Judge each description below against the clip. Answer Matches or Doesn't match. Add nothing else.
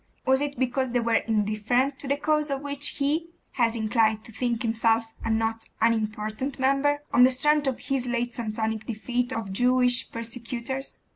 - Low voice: Doesn't match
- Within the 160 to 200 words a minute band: Matches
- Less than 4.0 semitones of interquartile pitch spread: Matches